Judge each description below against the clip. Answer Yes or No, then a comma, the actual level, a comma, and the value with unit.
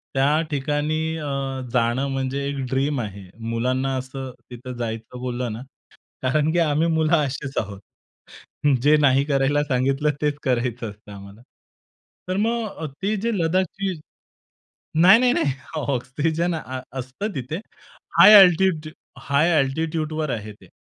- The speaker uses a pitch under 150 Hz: Yes, medium, 140 Hz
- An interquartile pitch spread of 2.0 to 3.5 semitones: No, average, 4.0 semitones